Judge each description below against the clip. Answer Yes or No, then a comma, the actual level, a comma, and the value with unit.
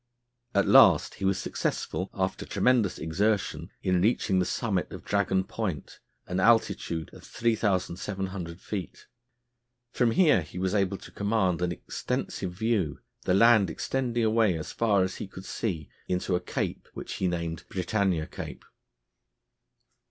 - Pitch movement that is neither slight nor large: Yes, average, 3.4 semitones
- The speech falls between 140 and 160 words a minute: Yes, average, 145 wpm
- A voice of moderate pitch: No, very low, 95 Hz